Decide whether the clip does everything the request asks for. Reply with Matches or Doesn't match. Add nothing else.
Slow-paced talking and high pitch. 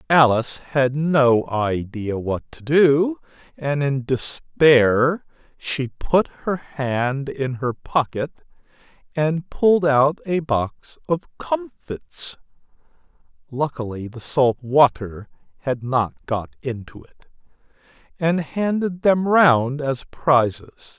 Doesn't match